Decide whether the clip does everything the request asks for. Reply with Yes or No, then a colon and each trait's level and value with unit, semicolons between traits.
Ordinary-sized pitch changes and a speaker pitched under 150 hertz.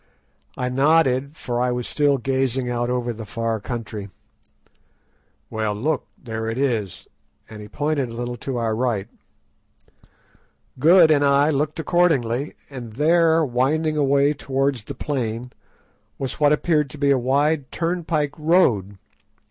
Yes: average, 4.0 semitones; low, 135 Hz